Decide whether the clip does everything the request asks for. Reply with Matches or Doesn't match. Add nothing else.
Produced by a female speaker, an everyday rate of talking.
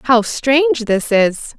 Matches